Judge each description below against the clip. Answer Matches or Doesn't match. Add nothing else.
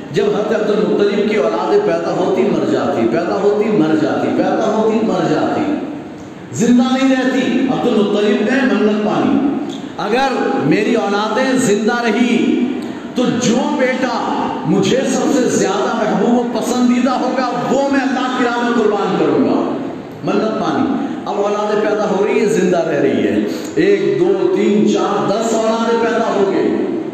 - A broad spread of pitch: Doesn't match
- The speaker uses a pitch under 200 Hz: Doesn't match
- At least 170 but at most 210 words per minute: Doesn't match